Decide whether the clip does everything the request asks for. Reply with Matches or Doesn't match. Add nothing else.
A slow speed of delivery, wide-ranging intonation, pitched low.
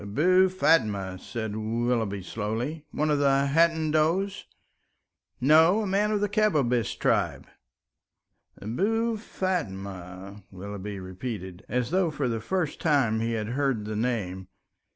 Matches